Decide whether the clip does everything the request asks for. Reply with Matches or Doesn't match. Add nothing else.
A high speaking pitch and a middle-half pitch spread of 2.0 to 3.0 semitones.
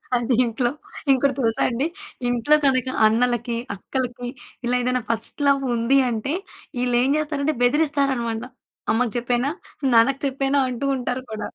Matches